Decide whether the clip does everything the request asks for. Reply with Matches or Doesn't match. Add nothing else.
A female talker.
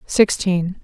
Matches